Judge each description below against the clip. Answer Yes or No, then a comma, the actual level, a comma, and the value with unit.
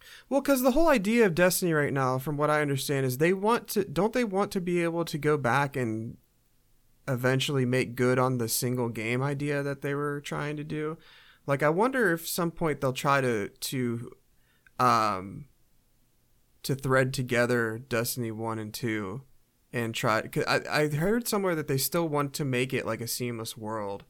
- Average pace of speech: Yes, average, 190 wpm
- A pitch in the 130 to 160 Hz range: Yes, low, 135 Hz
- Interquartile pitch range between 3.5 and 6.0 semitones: Yes, average, 5.2 semitones